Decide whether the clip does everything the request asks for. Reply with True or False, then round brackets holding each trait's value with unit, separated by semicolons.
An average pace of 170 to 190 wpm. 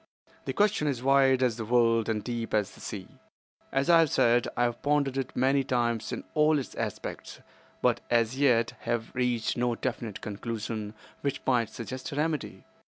True (180 wpm)